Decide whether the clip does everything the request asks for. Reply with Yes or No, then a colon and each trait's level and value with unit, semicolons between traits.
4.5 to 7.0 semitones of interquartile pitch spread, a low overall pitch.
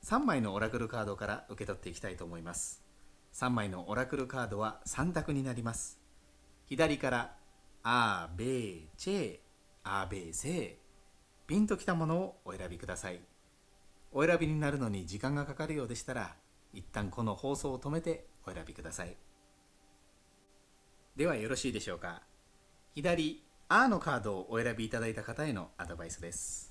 Yes: average, 5.3 semitones; low, 100 Hz